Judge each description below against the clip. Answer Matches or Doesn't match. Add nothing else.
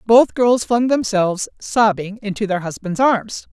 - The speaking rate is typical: Matches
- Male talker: Doesn't match